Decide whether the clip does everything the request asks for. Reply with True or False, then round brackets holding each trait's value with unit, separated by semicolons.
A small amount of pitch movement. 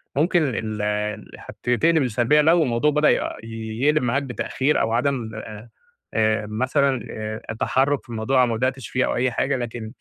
False (4.0 semitones)